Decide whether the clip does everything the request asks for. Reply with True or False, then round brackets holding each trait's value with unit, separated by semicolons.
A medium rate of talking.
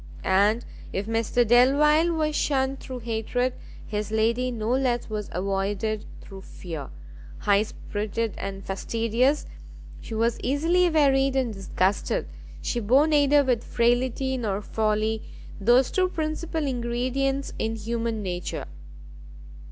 False (120 wpm)